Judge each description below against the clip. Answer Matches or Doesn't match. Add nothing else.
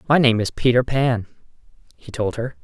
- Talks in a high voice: Doesn't match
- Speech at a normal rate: Matches